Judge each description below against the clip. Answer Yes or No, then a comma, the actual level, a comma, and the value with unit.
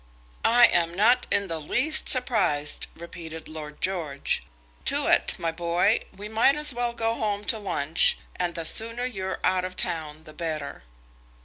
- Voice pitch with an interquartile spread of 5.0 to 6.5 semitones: Yes, wide, 5.6 semitones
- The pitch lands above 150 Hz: Yes, medium, 185 Hz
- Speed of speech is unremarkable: Yes, average, 155 wpm